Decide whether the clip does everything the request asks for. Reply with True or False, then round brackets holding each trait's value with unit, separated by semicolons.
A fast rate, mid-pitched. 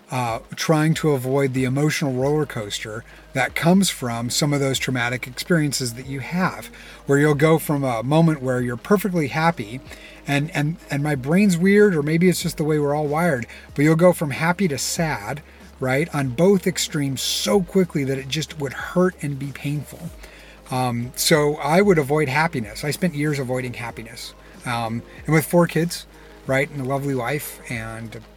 False (185 wpm; 145 Hz)